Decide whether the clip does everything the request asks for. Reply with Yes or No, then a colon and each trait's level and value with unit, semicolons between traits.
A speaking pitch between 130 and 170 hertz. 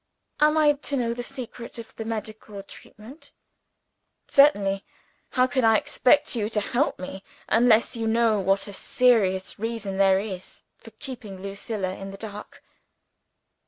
No: high, 220 Hz